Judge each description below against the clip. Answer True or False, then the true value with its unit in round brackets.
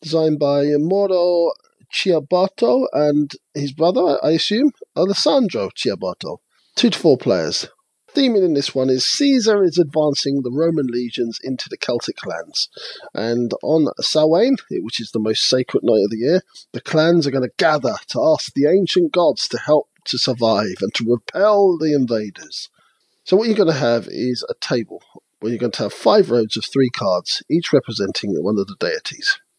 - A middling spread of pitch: False (6.4 semitones)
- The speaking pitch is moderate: True (150 Hz)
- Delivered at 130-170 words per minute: False (180 wpm)